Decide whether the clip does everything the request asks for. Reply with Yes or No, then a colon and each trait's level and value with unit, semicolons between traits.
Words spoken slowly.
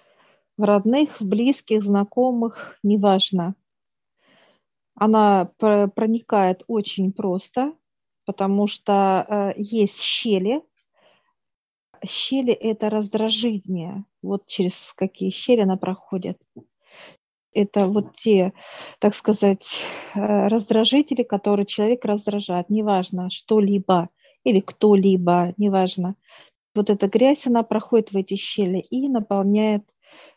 Yes: slow, 95 wpm